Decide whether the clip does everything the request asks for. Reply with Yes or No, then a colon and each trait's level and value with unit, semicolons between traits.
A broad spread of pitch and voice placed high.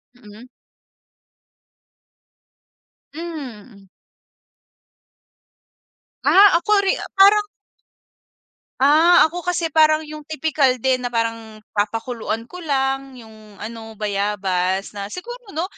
Yes: wide, 6.9 semitones; very high, 260 Hz